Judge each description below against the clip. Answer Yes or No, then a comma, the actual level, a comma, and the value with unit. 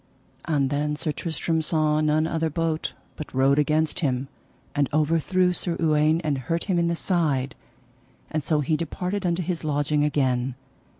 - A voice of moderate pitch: Yes, medium, 155 Hz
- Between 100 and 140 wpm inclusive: No, average, 165 wpm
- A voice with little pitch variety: Yes, narrow, 2.3 semitones